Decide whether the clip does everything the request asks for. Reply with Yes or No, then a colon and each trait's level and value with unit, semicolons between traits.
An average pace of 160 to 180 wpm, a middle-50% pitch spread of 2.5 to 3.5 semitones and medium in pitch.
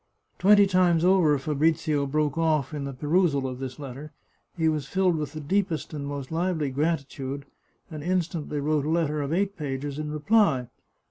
Yes: average, 175 wpm; average, 3.1 semitones; medium, 150 Hz